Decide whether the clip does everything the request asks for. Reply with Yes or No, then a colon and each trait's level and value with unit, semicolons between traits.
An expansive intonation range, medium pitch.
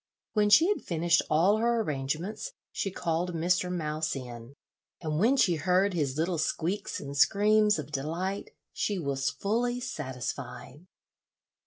Yes: wide, 5.7 semitones; medium, 170 Hz